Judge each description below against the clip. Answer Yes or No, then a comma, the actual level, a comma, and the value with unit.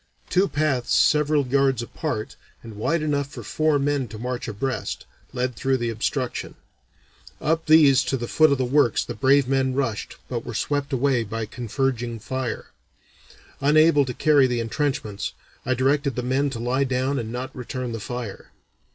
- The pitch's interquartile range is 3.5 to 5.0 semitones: No, average, 2.9 semitones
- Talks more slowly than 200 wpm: Yes, average, 175 wpm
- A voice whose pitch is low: Yes, low, 130 Hz